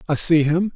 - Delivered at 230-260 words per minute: Yes, fast, 240 wpm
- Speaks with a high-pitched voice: No, medium, 165 Hz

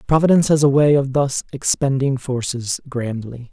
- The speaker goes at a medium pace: Yes, average, 155 wpm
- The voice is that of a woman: No, male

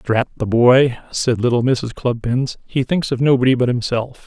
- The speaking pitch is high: No, low, 125 Hz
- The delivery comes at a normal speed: Yes, average, 185 wpm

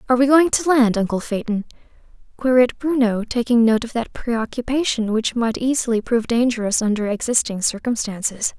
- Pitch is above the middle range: Yes, high, 235 Hz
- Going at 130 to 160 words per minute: Yes, average, 155 wpm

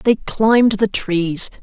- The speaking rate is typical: Yes, average, 150 wpm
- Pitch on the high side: Yes, high, 205 Hz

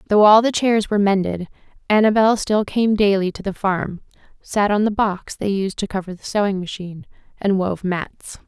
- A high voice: Yes, high, 200 Hz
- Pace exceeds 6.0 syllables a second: No, 5.1 syllables/s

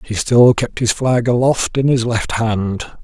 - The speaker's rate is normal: Yes, average, 195 wpm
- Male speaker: Yes, male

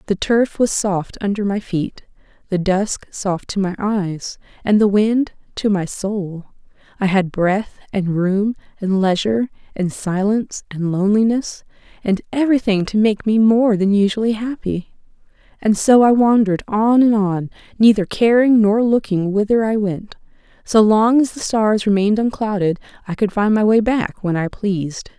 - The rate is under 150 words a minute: No, average, 165 wpm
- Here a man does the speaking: No, female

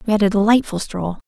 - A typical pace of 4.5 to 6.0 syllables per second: No, 6.5 syllables/s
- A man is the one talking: No, female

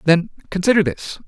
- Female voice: No, male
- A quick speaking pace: No, average, 140 wpm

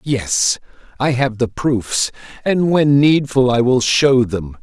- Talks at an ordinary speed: Yes, average, 155 wpm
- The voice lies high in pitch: No, low, 125 Hz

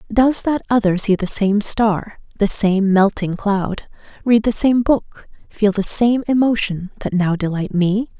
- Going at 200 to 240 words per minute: No, average, 170 wpm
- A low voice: No, high, 210 Hz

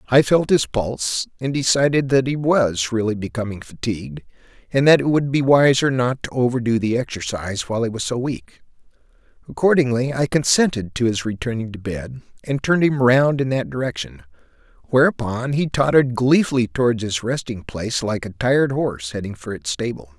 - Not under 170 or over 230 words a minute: Yes, average, 175 wpm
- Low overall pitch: Yes, low, 120 Hz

